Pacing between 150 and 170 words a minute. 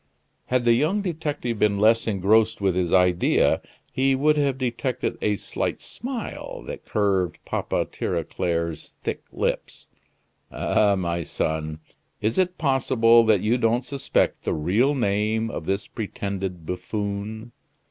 No: slow, 135 wpm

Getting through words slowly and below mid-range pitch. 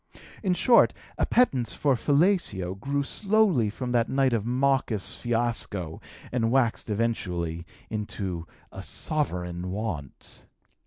Yes: slow, 115 wpm; low, 115 Hz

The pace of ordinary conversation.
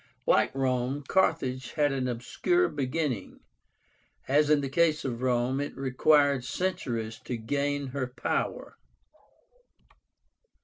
No: slow, 115 wpm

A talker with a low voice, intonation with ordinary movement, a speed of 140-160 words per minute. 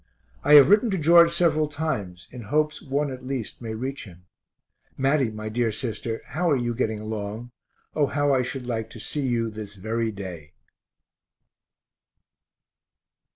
Yes: low, 125 Hz; average, 5.0 semitones; average, 155 wpm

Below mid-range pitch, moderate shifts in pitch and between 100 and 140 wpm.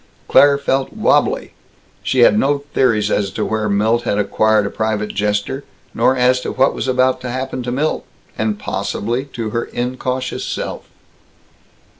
No: low, 120 Hz; average, 3.4 semitones; average, 160 wpm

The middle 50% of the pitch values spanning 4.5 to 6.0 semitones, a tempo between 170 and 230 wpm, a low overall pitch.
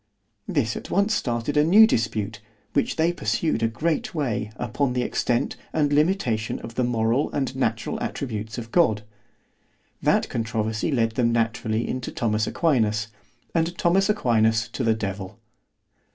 No: average, 5.0 semitones; average, 145 wpm; low, 120 Hz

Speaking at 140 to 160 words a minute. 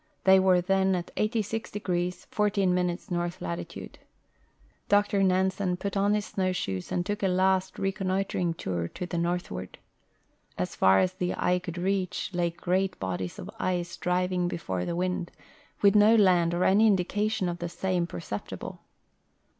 Yes: average, 150 wpm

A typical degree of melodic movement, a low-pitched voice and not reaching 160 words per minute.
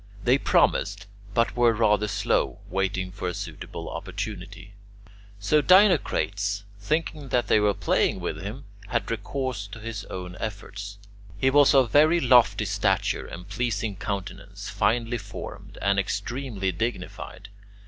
Yes: average, 3.7 semitones; low, 105 Hz; slow, 135 wpm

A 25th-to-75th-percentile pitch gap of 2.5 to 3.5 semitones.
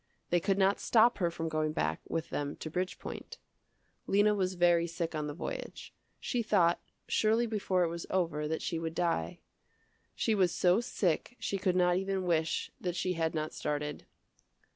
Yes: average, 3.1 semitones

